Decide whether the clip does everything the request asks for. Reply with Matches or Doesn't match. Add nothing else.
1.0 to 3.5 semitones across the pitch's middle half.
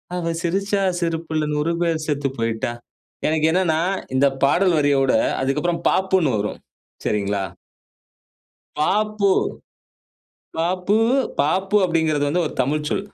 Doesn't match